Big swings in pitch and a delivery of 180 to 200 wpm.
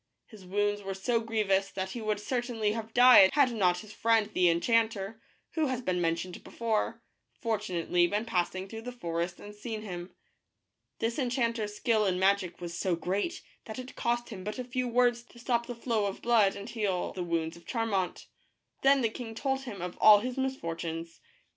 No: average, 4.1 semitones; average, 190 wpm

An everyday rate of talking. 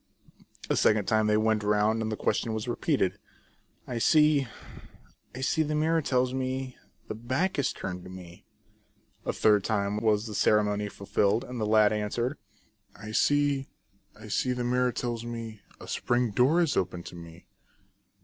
Yes: average, 175 wpm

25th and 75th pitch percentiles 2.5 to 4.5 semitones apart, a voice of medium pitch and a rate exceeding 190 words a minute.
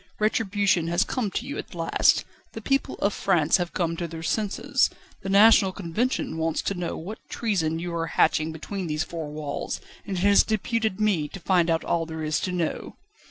Yes: average, 3.8 semitones; medium, 175 Hz; average, 200 wpm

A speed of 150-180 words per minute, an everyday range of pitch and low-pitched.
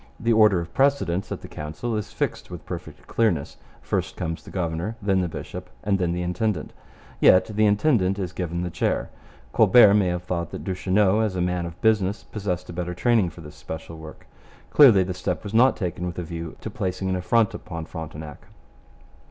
No: average, 200 wpm; average, 3.6 semitones; very low, 90 Hz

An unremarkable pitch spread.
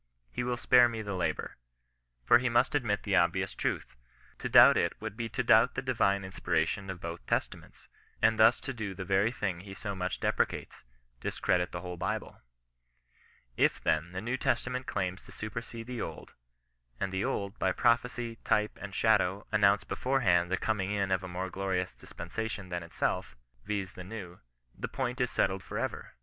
Yes: average, 3.7 semitones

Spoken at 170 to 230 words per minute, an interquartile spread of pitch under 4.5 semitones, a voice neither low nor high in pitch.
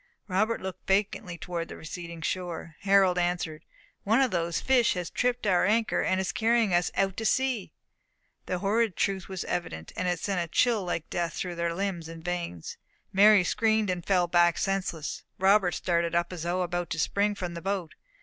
Yes: average, 190 wpm; average, 2.7 semitones; medium, 180 Hz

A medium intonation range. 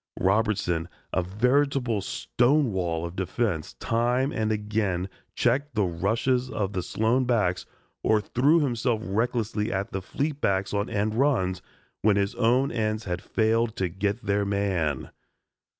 Yes: average, 4.1 semitones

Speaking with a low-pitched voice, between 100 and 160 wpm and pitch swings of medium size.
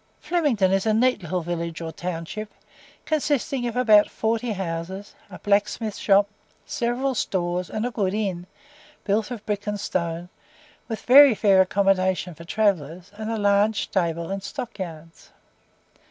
No: high, 200 Hz; average, 155 wpm; average, 3.7 semitones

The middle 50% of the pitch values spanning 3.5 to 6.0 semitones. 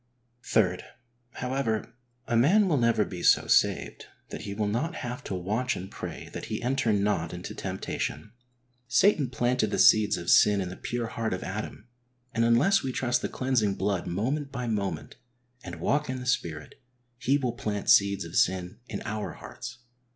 Yes: average, 4.3 semitones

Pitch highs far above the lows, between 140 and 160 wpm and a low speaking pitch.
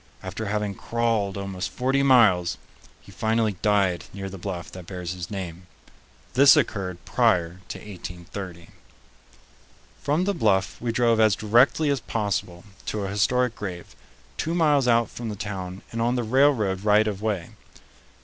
No: average, 4.1 semitones; average, 155 wpm; low, 105 Hz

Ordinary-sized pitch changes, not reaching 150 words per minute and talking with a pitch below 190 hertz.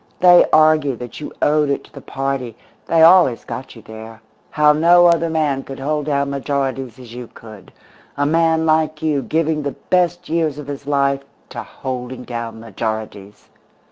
No: average, 4.1 semitones; average, 175 wpm; medium, 140 Hz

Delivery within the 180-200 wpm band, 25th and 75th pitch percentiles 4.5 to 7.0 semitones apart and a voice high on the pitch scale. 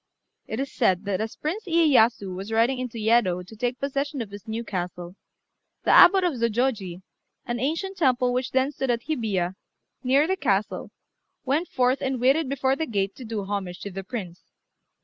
Yes: average, 185 wpm; average, 5.2 semitones; high, 240 Hz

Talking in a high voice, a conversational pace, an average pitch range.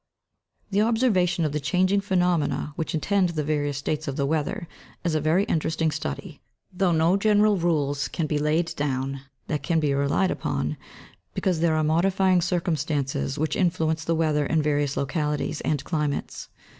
No: medium, 160 Hz; average, 165 wpm; average, 3.4 semitones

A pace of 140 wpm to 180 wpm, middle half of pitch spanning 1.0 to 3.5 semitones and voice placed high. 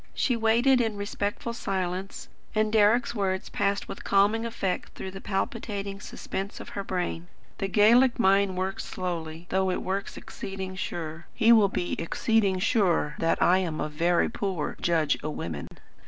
Yes: average, 160 wpm; average, 3.2 semitones; high, 195 Hz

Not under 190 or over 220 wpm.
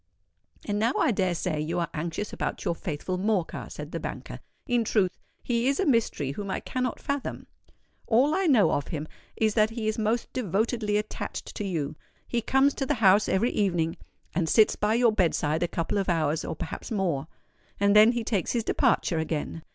Yes: average, 200 wpm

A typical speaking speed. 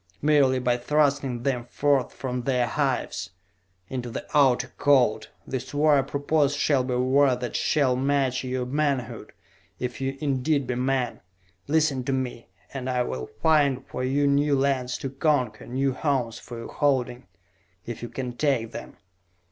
Yes: average, 165 wpm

